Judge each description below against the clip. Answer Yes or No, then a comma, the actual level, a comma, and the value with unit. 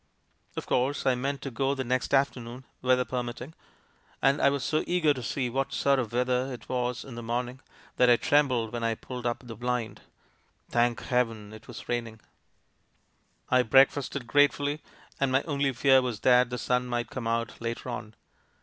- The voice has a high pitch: No, low, 125 Hz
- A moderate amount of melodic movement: No, narrow, 2.2 semitones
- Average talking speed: Yes, average, 195 wpm